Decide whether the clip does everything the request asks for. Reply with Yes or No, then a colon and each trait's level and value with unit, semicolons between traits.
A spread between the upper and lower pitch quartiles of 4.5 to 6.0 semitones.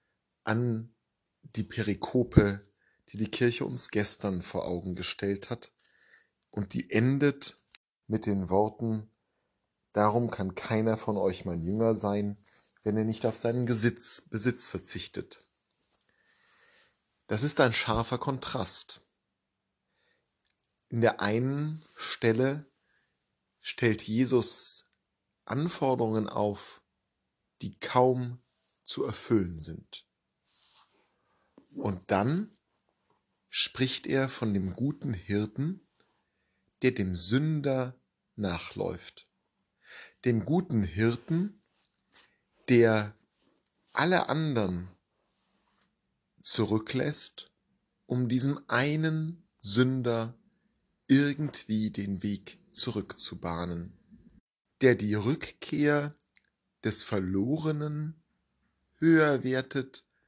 Yes: average, 4.8 semitones